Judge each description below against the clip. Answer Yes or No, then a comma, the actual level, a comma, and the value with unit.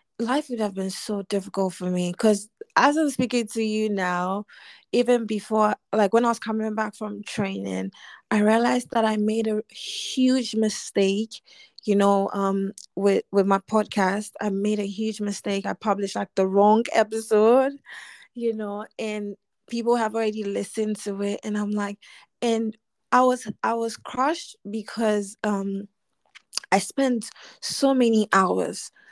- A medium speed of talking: Yes, average, 155 wpm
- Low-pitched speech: No, high, 215 Hz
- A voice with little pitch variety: Yes, narrow, 2.3 semitones